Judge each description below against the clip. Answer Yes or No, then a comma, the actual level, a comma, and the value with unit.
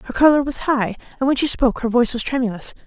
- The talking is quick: Yes, fast, 250 wpm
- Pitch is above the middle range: Yes, very high, 250 Hz